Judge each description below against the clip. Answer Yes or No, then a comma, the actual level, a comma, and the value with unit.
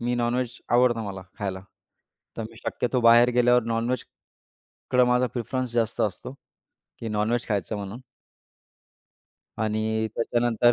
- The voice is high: No, low, 115 Hz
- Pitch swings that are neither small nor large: No, narrow, 2.0 semitones